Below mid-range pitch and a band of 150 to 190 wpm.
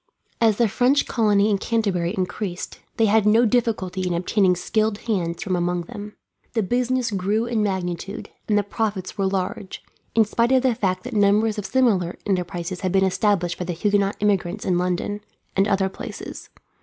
No: high, 200 Hz; average, 180 wpm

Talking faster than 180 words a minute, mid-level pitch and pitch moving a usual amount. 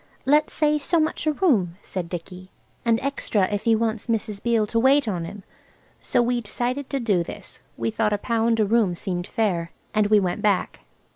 No: average, 200 wpm; high, 220 Hz; average, 3.8 semitones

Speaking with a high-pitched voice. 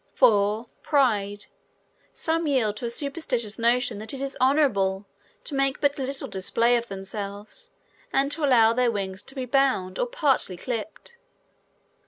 Yes: high, 245 Hz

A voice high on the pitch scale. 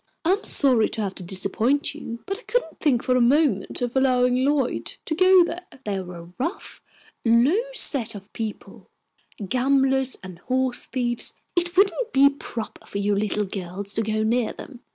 Yes: very high, 250 Hz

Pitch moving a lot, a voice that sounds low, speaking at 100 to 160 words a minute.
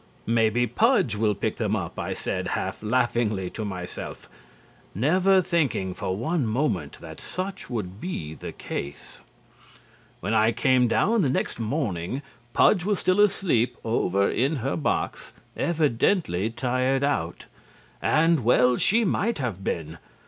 Yes: wide, 7.7 semitones; low, 120 Hz; average, 140 wpm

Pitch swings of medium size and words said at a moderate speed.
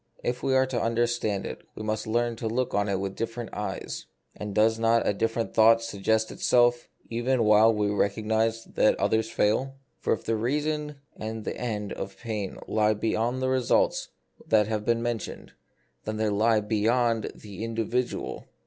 No: narrow, 1.9 semitones; average, 175 wpm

